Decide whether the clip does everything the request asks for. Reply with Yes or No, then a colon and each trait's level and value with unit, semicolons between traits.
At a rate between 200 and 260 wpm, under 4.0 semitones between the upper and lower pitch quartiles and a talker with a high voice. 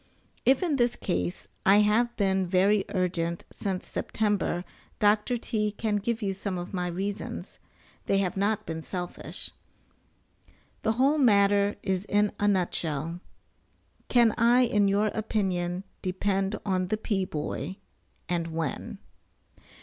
No: slow, 135 wpm; average, 2.9 semitones; high, 200 Hz